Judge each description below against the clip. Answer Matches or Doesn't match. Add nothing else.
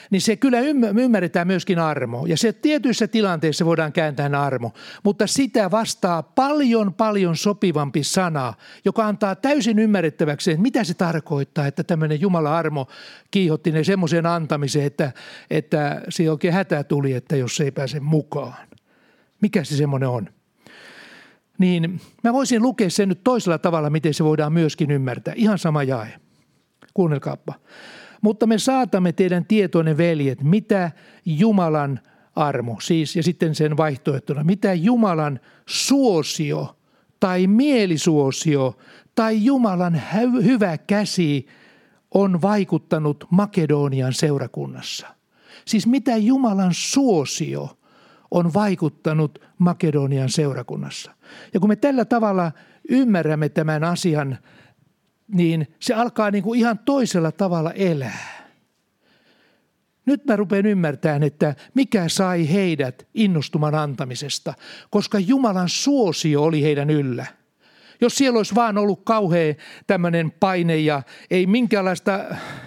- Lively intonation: Matches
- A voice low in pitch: Doesn't match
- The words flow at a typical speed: Matches